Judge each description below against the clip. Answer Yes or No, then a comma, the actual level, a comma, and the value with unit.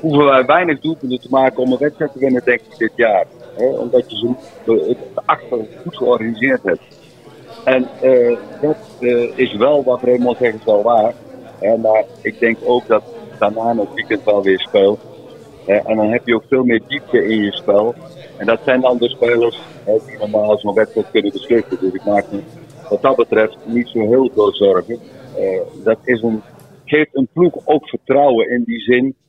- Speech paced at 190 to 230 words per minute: Yes, average, 195 wpm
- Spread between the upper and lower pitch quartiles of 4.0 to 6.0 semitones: No, average, 3.4 semitones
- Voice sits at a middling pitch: No, low, 125 Hz